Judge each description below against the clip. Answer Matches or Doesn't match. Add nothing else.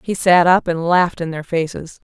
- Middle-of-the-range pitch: Matches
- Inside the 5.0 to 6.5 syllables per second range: Matches